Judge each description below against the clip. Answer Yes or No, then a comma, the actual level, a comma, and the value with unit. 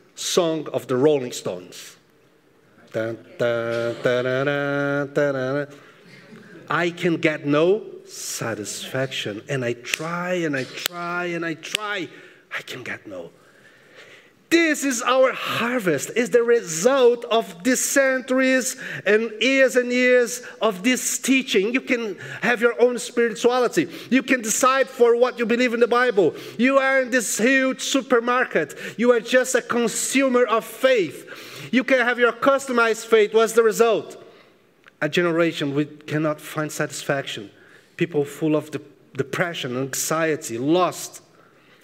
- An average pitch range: No, wide, 8.7 semitones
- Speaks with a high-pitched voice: Yes, high, 225 Hz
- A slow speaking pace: Yes, slow, 130 wpm